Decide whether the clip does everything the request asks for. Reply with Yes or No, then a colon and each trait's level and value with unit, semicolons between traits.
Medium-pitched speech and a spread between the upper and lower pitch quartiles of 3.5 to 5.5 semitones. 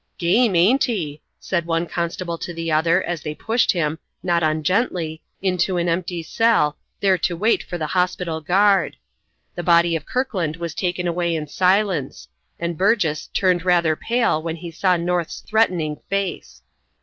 No: medium, 175 Hz; narrow, 2.5 semitones